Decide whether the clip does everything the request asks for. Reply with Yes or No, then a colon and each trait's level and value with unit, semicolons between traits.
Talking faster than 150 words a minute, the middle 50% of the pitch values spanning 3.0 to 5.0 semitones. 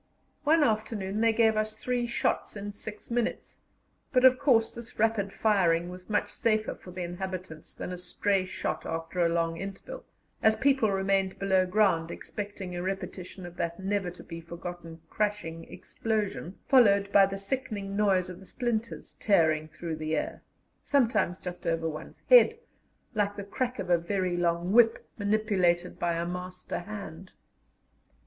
Yes: average, 160 wpm; average, 3.6 semitones